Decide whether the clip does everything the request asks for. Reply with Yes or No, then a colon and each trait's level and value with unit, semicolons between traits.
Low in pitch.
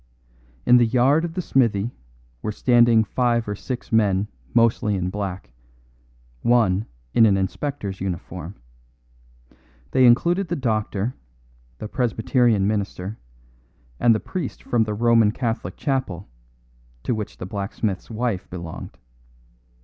Yes: low, 110 Hz